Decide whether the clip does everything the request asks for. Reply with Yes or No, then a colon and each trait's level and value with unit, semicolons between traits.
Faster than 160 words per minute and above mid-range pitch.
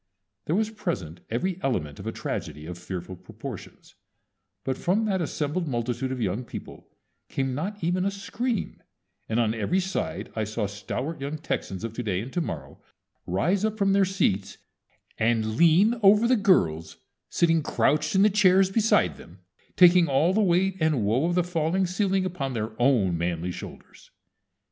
No: average, 170 wpm; medium, 155 Hz